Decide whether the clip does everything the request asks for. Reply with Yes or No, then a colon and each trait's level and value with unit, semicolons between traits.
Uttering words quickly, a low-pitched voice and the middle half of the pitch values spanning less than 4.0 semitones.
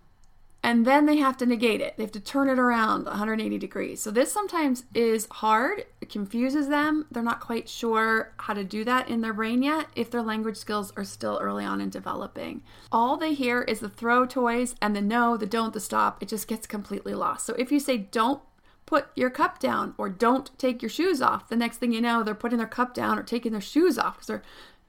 No: fast, 230 wpm; high, 235 Hz; average, 3.2 semitones